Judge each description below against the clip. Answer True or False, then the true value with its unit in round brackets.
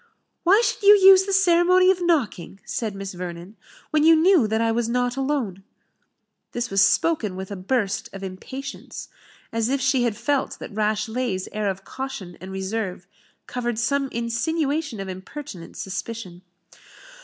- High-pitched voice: True (235 Hz)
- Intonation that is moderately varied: False (6.9 semitones)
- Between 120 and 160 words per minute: True (155 wpm)